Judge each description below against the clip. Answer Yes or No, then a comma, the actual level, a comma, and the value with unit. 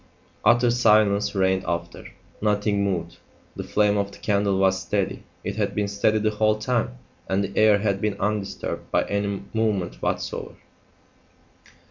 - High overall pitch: No, low, 100 Hz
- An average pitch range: No, narrow, 1.7 semitones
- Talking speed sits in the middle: Yes, average, 150 wpm